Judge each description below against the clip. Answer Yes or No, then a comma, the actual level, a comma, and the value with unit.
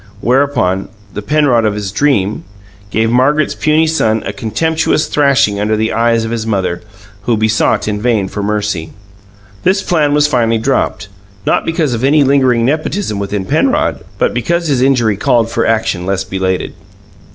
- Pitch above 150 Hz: No, low, 115 Hz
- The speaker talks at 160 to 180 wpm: Yes, average, 165 wpm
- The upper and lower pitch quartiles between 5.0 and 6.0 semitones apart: Yes, wide, 5.5 semitones